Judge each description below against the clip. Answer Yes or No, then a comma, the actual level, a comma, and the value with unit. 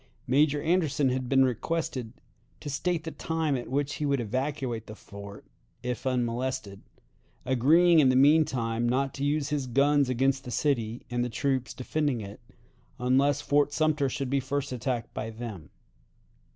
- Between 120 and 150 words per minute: No, average, 165 wpm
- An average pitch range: Yes, average, 3.1 semitones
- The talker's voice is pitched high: No, low, 135 Hz